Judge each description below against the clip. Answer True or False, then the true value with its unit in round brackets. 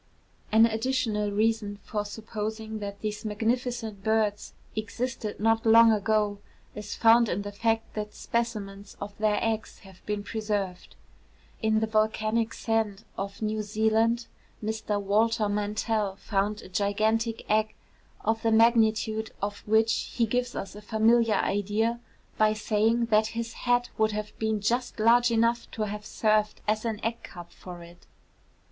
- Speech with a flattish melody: True (1.4 semitones)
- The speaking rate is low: False (150 wpm)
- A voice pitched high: True (220 Hz)